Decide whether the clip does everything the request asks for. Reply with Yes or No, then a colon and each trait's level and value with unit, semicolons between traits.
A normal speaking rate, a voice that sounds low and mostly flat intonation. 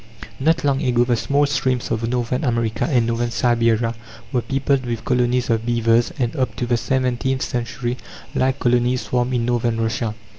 Yes: average, 175 wpm; low, 120 Hz; narrow, 1.7 semitones